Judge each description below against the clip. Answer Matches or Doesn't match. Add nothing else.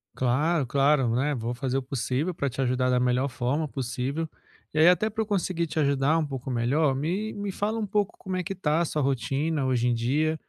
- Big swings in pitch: Doesn't match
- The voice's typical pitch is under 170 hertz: Matches